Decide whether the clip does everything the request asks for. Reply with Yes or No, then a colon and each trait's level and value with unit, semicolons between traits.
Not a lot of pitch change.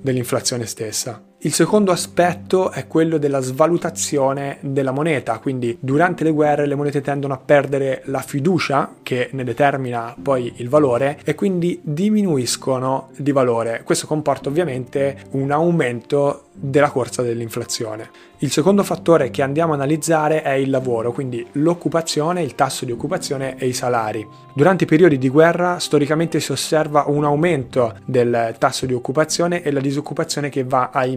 No: average, 3.5 semitones